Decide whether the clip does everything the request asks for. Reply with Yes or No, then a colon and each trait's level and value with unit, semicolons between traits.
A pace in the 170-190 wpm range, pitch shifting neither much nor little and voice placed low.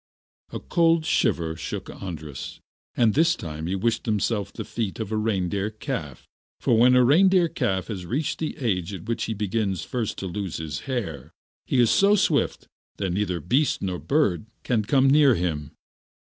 No: average, 175 wpm; wide, 6.1 semitones; low, 110 Hz